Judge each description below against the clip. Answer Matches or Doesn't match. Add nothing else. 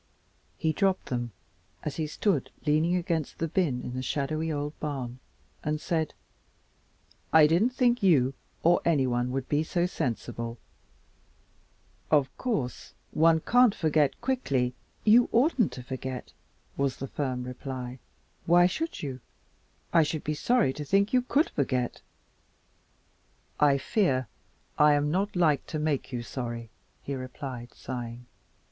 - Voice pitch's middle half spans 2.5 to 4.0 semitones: Doesn't match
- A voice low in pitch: Doesn't match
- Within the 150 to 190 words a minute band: Doesn't match